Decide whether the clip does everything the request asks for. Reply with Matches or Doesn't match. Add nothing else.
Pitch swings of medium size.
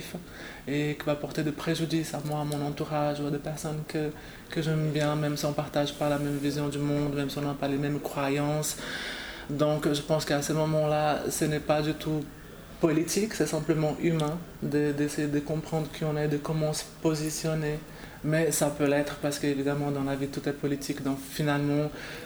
Doesn't match